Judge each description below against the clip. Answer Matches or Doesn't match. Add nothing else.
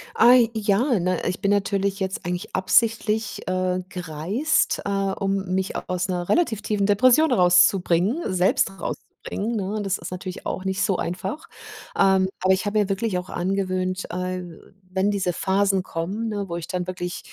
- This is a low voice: Doesn't match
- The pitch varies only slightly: Matches